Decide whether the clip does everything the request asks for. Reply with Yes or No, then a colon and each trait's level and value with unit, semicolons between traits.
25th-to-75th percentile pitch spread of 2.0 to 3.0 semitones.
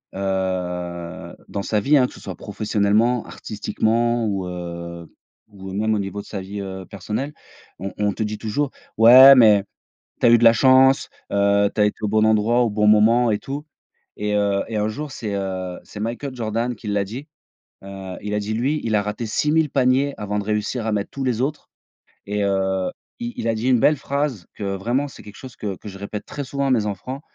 No: average, 3.6 semitones